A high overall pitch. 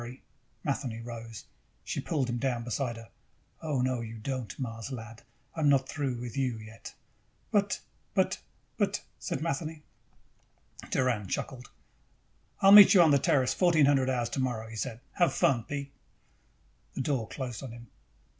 No: low, 130 Hz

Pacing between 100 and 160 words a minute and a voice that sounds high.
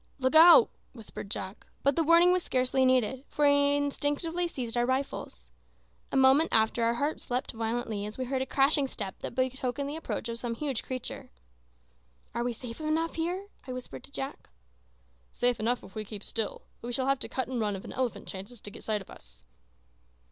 No: average, 200 wpm; very high, 255 Hz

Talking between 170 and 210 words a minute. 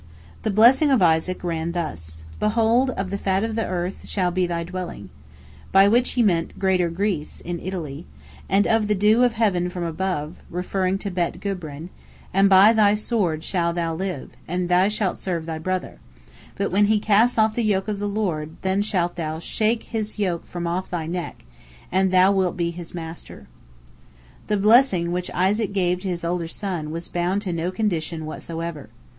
Yes: average, 185 wpm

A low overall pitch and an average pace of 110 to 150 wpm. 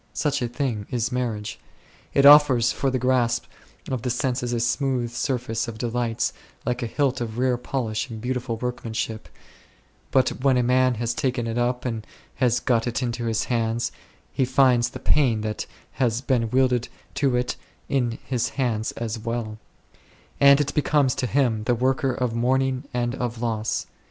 No: low, 125 Hz; average, 175 wpm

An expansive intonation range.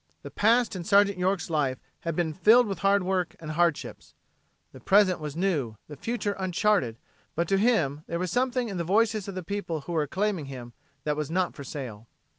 No: average, 4.8 semitones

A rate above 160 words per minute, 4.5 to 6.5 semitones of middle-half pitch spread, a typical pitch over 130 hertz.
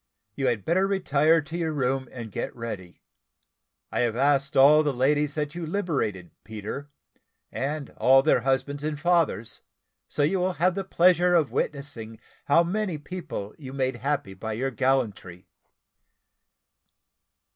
No: average, 145 wpm; average, 4.8 semitones; medium, 140 Hz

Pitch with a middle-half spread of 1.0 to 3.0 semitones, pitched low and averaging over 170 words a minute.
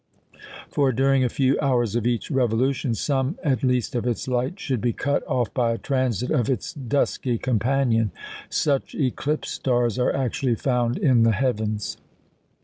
No: narrow, 2.4 semitones; low, 125 Hz; average, 160 wpm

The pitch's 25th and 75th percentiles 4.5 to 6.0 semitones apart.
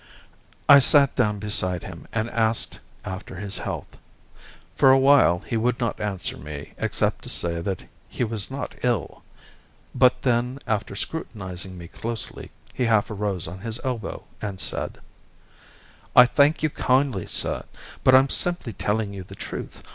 Yes: average, 4.9 semitones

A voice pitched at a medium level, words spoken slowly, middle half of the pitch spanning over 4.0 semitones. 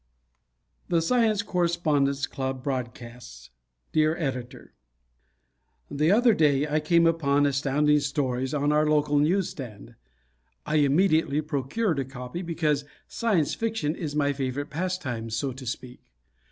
No: medium, 145 Hz; slow, 125 wpm; average, 3.7 semitones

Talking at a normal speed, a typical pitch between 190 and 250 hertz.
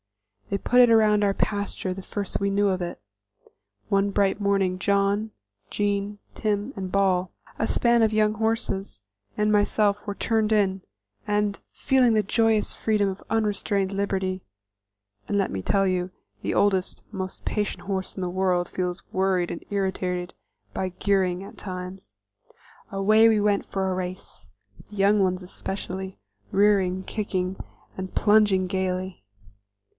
Yes: average, 150 wpm; high, 195 Hz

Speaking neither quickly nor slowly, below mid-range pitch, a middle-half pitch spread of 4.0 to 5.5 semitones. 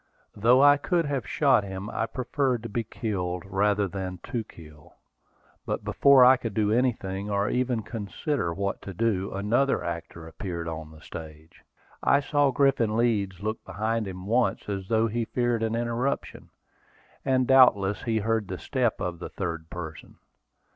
Yes: average, 165 wpm; low, 110 Hz; average, 4.3 semitones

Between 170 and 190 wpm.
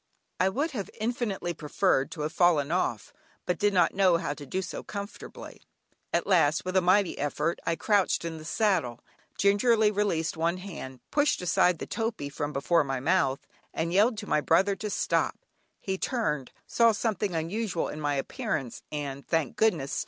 Yes: average, 175 wpm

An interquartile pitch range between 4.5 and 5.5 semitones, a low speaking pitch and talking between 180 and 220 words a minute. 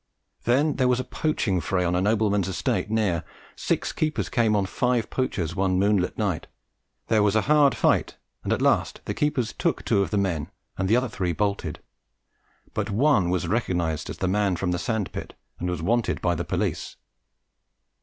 Yes: average, 4.8 semitones; low, 100 Hz; average, 190 wpm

